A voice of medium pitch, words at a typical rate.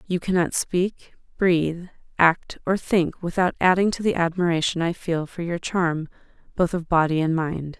Yes: medium, 170 Hz; average, 170 wpm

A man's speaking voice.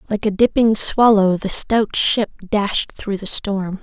No: female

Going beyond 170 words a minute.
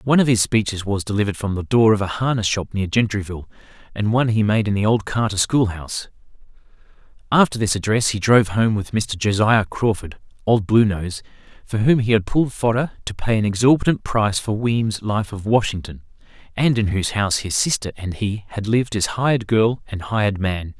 Yes: average, 195 wpm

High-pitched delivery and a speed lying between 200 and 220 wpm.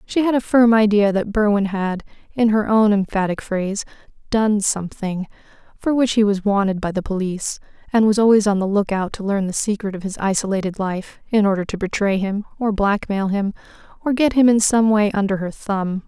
Yes: high, 205 Hz; fast, 205 wpm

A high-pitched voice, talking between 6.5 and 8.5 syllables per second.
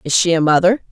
No: medium, 175 Hz; 6.6 syllables/s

